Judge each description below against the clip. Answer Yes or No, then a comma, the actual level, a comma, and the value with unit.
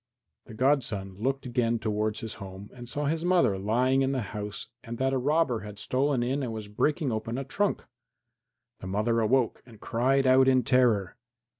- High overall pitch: No, low, 120 Hz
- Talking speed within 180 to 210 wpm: Yes, average, 185 wpm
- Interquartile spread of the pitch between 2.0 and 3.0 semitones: No, average, 3.7 semitones